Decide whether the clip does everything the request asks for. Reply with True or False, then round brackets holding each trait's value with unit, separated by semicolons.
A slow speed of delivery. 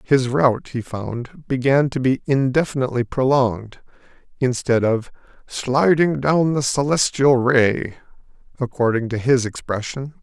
True (115 wpm)